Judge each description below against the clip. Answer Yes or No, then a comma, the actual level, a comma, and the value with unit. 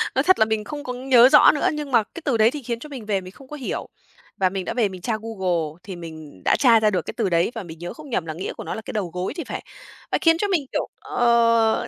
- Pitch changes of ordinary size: No, wide, 6.0 semitones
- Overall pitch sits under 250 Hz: Yes, high, 225 Hz